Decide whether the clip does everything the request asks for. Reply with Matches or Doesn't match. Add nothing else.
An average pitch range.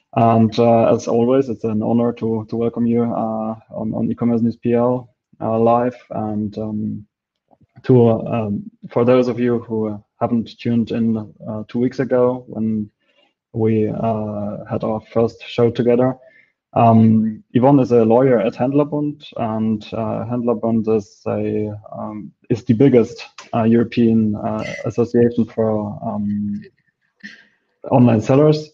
Doesn't match